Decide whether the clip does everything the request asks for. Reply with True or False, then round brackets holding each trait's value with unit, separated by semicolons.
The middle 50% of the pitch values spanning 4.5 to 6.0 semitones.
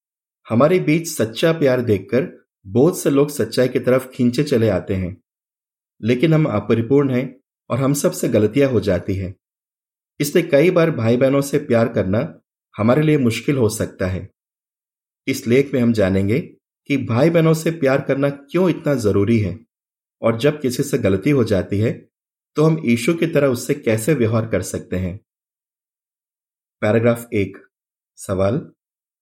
True (5.1 semitones)